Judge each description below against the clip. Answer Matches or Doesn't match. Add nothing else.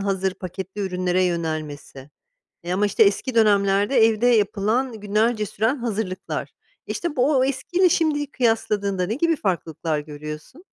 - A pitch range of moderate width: Matches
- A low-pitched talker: Doesn't match